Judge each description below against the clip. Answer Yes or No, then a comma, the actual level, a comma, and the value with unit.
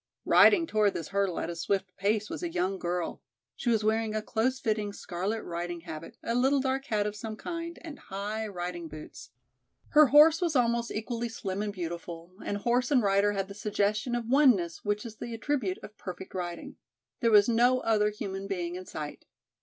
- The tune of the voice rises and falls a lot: No, average, 4.2 semitones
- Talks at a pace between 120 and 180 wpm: No, average, 195 wpm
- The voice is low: No, high, 210 Hz